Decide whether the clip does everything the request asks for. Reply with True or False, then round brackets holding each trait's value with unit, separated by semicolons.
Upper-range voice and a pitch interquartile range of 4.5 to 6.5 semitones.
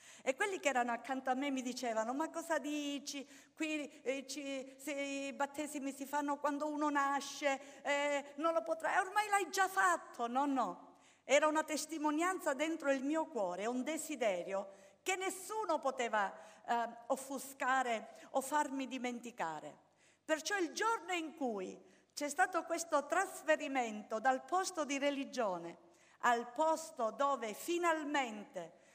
False (285 Hz; 3.5 semitones)